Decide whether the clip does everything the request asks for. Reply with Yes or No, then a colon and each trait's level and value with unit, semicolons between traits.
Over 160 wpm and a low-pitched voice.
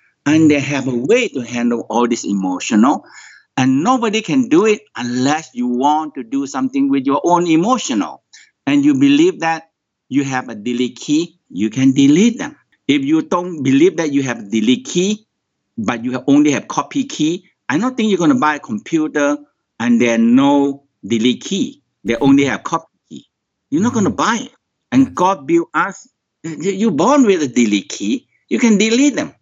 No: average, 190 wpm; medium, 155 Hz